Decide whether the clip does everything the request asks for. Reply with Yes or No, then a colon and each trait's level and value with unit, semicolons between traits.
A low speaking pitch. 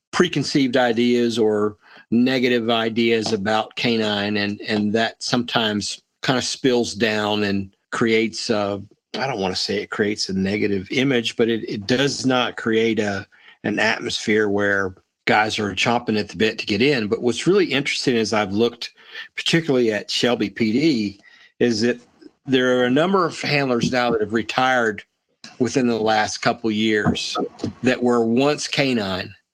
Yes: low, 115 Hz